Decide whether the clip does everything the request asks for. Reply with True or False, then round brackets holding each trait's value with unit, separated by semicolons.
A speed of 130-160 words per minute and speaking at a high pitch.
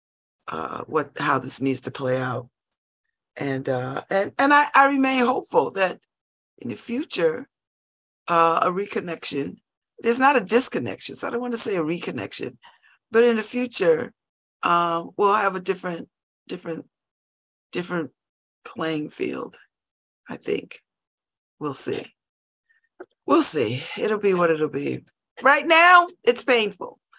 True (140 wpm; 205 Hz)